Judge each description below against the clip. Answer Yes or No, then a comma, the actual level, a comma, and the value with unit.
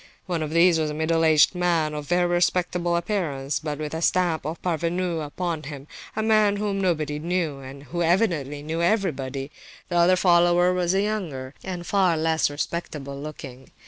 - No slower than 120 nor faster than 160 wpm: No, average, 175 wpm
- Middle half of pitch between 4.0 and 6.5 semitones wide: No, average, 3.0 semitones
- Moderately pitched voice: Yes, medium, 170 Hz